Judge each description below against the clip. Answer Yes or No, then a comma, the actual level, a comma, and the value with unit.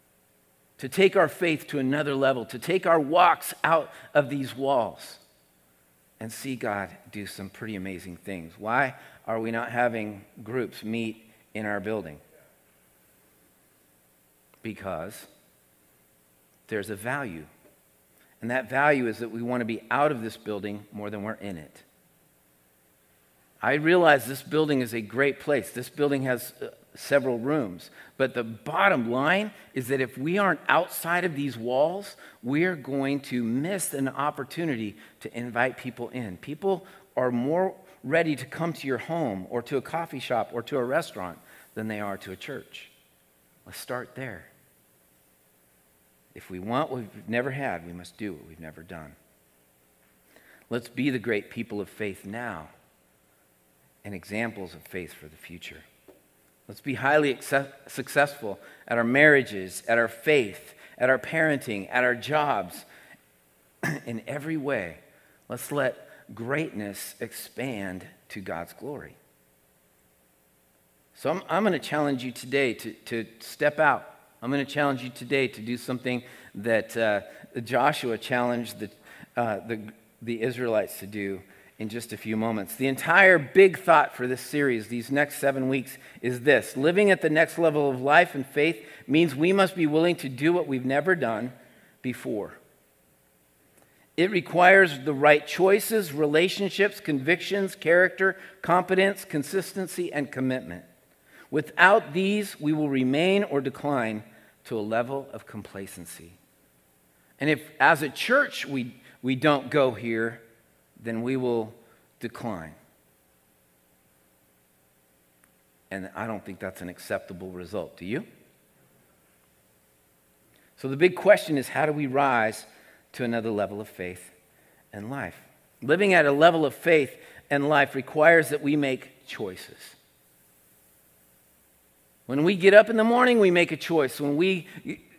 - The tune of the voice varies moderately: No, wide, 8.7 semitones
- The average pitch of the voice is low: Yes, low, 120 Hz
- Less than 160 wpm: Yes, average, 150 wpm